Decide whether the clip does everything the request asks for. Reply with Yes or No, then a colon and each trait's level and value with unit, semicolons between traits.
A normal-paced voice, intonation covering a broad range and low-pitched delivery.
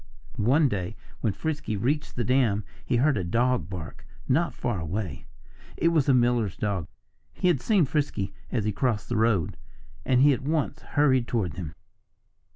Yes: average, 170 wpm; wide, 5.8 semitones; low, 120 Hz